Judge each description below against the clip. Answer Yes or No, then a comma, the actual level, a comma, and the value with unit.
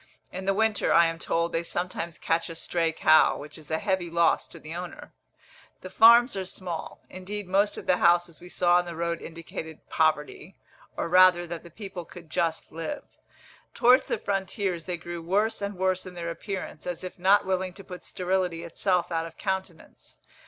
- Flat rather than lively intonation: Yes, narrow, 2.2 semitones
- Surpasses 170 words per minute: Yes, average, 195 wpm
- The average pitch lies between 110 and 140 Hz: No, medium, 175 Hz